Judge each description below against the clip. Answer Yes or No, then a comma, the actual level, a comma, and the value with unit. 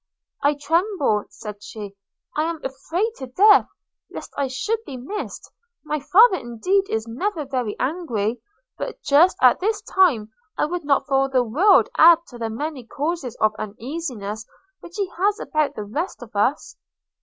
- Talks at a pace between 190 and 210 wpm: No, average, 165 wpm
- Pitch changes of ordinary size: No, wide, 6.8 semitones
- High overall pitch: Yes, very high, 280 Hz